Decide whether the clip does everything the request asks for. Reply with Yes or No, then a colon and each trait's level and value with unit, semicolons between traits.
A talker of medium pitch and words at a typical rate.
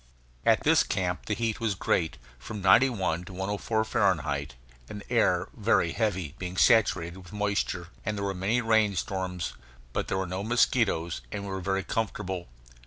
No: very low, 95 Hz; average, 175 wpm